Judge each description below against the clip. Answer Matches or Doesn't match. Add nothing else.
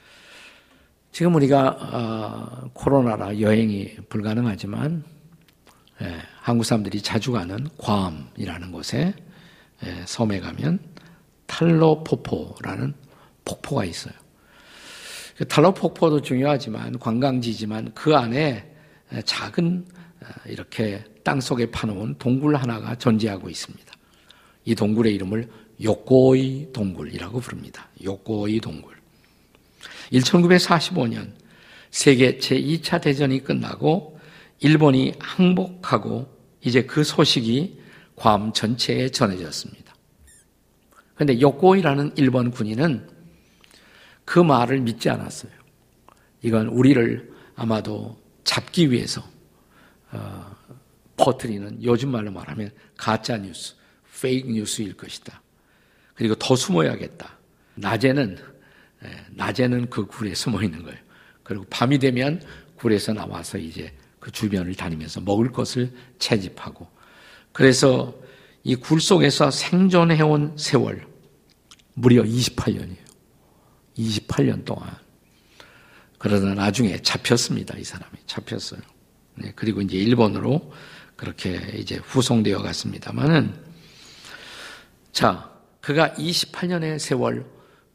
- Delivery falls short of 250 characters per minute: Matches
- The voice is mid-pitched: Doesn't match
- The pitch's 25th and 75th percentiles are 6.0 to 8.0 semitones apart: Doesn't match